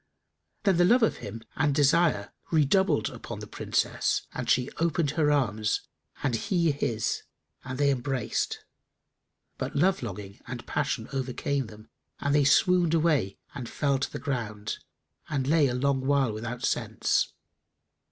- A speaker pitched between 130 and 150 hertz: Yes, medium, 140 Hz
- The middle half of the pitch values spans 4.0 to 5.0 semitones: Yes, average, 4.3 semitones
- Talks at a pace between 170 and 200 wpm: No, average, 150 wpm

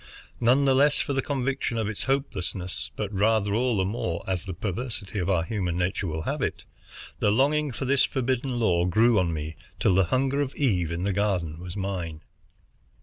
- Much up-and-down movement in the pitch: Yes, wide, 6.1 semitones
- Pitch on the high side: No, low, 105 Hz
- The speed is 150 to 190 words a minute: No, average, 200 wpm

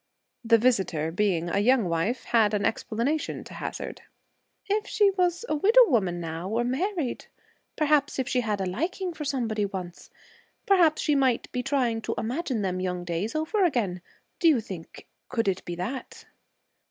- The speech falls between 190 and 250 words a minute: No, average, 165 wpm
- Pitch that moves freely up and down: Yes, wide, 8.1 semitones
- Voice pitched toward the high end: Yes, high, 235 Hz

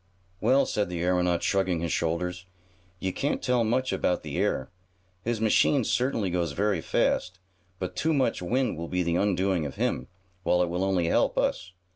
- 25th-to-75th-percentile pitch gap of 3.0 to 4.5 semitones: Yes, average, 4.1 semitones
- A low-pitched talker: Yes, very low, 90 Hz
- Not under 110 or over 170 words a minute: No, average, 180 wpm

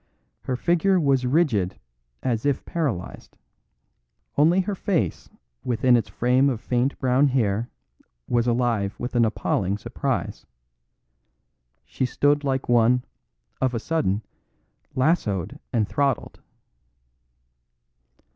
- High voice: No, low, 125 Hz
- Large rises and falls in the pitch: No, average, 3.7 semitones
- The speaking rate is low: Yes, slow, 110 wpm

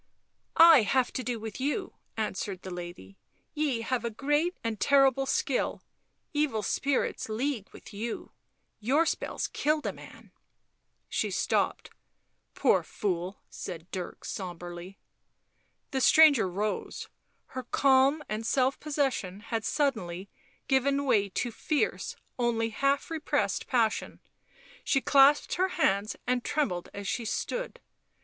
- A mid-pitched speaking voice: No, high, 245 Hz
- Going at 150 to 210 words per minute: No, slow, 135 wpm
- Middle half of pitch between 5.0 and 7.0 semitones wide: Yes, wide, 5.6 semitones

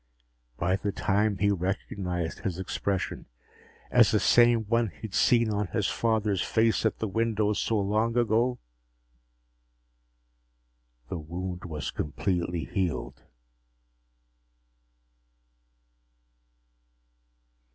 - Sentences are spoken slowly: Yes, slow, 95 wpm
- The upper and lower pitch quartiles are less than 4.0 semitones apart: Yes, average, 3.6 semitones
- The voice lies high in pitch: No, low, 100 Hz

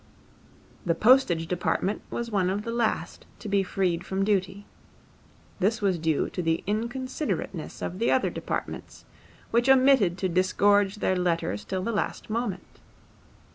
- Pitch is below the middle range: No, high, 195 Hz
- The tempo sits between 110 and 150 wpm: Yes, average, 145 wpm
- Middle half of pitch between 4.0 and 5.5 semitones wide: Yes, average, 4.3 semitones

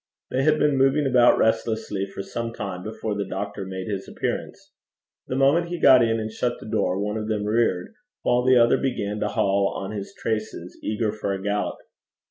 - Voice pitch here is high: No, low, 110 Hz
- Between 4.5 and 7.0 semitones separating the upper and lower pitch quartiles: No, average, 3.4 semitones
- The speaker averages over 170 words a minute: Yes, average, 200 wpm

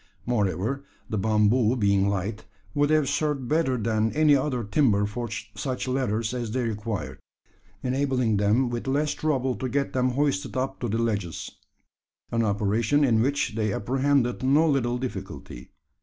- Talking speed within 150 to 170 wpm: Yes, average, 155 wpm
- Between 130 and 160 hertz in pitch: No, low, 120 Hz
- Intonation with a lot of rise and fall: No, average, 4.0 semitones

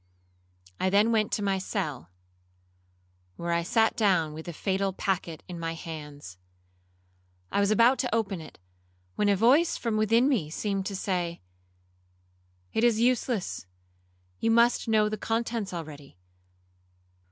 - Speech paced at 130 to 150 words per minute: Yes, average, 140 wpm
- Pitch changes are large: Yes, wide, 6.2 semitones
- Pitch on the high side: Yes, high, 195 Hz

